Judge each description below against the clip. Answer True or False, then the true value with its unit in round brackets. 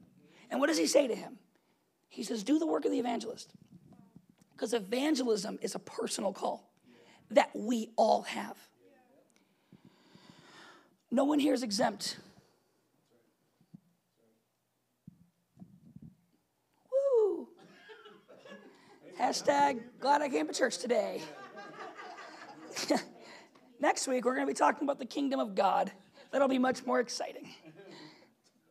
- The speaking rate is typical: False (115 wpm)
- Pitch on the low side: False (245 Hz)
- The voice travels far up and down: True (6.8 semitones)